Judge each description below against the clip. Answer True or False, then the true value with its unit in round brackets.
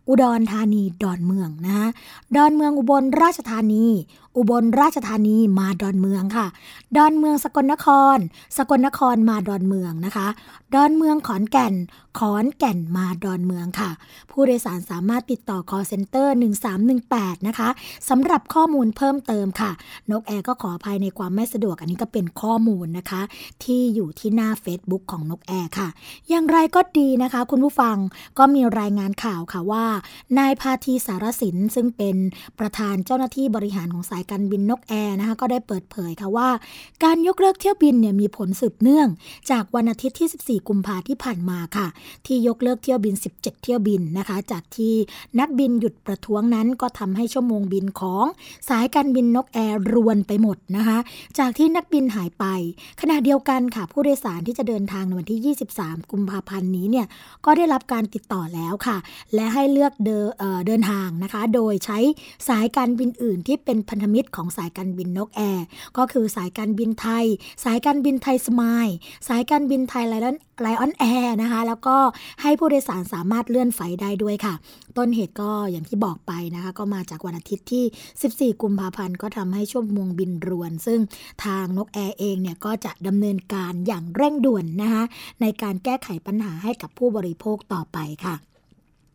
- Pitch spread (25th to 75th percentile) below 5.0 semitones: True (4.5 semitones)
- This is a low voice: False (220 Hz)